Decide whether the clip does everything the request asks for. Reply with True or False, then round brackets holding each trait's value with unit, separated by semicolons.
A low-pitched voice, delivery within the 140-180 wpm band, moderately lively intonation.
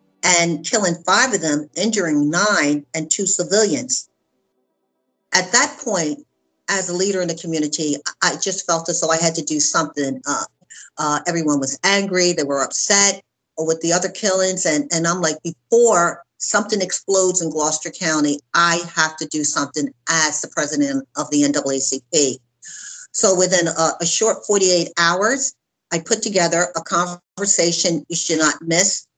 False (170 Hz; 160 wpm; 4.0 semitones)